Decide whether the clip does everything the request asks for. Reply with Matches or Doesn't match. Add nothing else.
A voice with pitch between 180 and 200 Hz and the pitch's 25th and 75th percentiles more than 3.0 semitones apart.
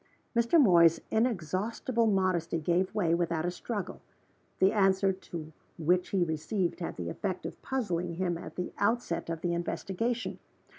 Matches